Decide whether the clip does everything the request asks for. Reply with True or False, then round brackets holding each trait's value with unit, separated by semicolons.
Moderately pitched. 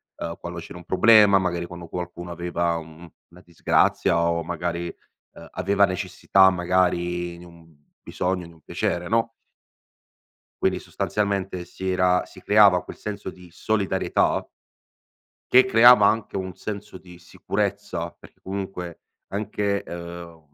False (90 Hz)